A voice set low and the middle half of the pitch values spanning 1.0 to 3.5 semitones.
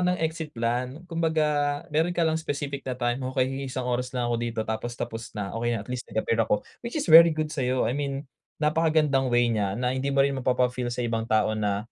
No: low, 130 Hz; average, 4.2 semitones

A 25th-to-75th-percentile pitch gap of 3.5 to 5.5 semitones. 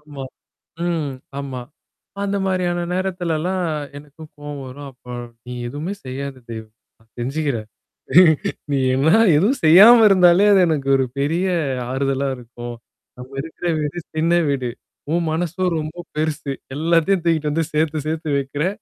Yes: average, 4.0 semitones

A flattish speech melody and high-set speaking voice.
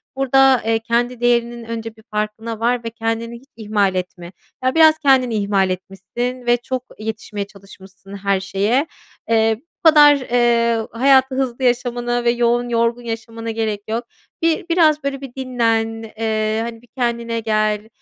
Yes: narrow, 2.1 semitones; high, 230 Hz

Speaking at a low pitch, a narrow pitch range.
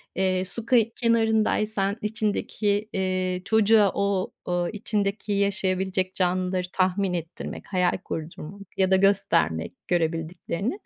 No: high, 190 Hz; narrow, 2.2 semitones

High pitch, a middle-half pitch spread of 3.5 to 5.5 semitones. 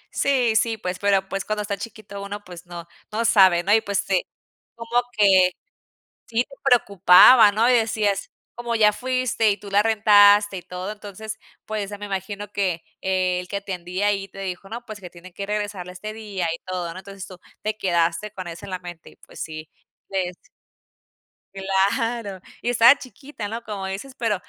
No: high, 200 Hz; average, 2.7 semitones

